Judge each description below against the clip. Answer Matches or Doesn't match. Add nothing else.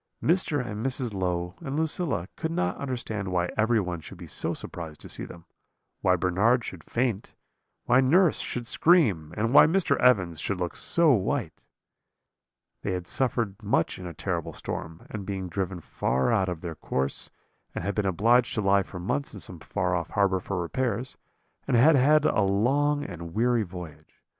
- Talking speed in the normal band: Matches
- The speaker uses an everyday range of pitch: Doesn't match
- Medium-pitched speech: Doesn't match